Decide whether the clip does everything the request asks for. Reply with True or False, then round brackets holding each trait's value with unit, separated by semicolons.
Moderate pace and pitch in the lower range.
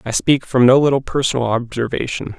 True (175 wpm; 130 Hz)